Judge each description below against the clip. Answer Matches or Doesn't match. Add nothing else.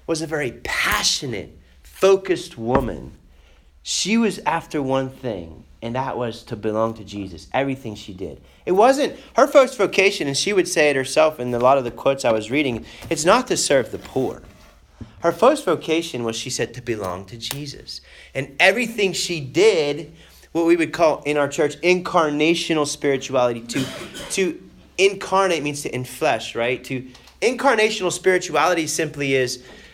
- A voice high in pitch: Doesn't match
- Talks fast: Doesn't match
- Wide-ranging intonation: Matches